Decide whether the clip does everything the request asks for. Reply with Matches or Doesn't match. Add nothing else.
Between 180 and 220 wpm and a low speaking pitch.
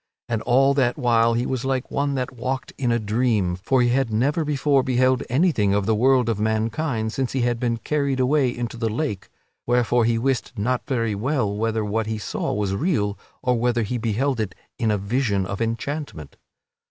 Matches